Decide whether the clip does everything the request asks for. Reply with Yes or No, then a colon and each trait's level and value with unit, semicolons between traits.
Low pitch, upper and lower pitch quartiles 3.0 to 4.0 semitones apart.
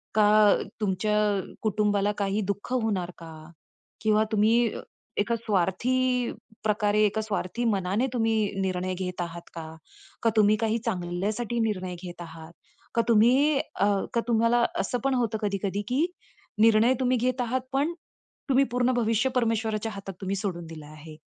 No: high, 215 Hz; average, 3.7 semitones